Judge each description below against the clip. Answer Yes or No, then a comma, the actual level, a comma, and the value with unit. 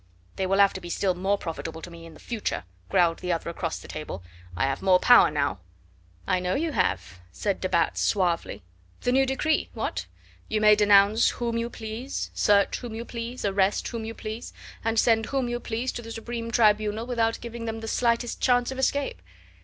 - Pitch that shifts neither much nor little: Yes, average, 4.3 semitones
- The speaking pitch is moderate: No, high, 220 Hz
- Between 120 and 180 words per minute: No, fast, 205 wpm